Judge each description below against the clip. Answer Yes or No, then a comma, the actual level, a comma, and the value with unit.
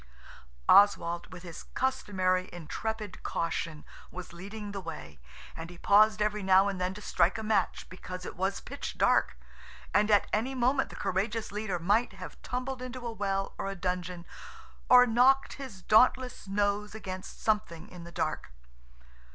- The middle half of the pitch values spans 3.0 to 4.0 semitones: Yes, average, 3.3 semitones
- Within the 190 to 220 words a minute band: No, average, 160 wpm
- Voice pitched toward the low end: No, high, 200 Hz